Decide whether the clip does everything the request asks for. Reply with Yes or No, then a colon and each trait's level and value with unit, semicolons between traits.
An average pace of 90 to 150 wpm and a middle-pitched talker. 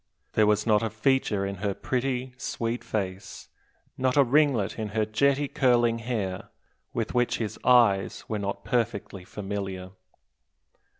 No: average, 140 wpm; low, 110 Hz